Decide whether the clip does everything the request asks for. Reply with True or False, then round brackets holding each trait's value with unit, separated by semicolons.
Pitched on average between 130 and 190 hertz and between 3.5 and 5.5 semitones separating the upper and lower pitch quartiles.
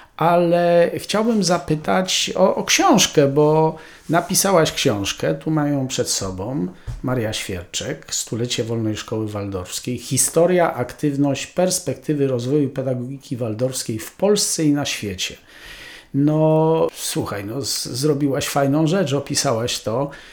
True (140 Hz; 4.6 semitones)